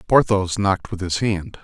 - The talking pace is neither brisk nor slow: Yes, average, 185 wpm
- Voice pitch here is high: No, very low, 95 Hz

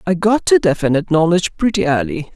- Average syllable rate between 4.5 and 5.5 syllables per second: No, 6.5 syllables/s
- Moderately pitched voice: Yes, medium, 170 Hz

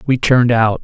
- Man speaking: Yes, male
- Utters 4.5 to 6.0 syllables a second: Yes, 5.8 syllables/s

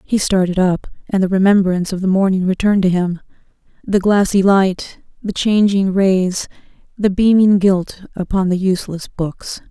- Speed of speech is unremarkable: Yes, average, 150 wpm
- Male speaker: No, female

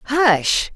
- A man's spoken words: No, female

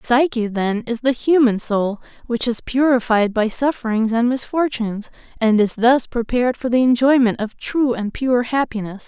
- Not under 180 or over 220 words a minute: No, average, 165 wpm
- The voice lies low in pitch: No, high, 240 Hz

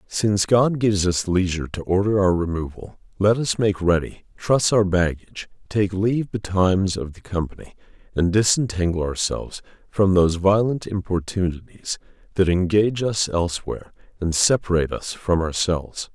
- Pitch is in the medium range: No, very low, 95 Hz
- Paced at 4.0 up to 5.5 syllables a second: Yes, 5.2 syllables/s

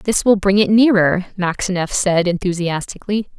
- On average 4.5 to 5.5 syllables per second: Yes, 5.0 syllables/s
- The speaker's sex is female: Yes, female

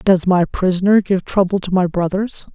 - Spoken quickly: No, average, 190 wpm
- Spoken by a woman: Yes, female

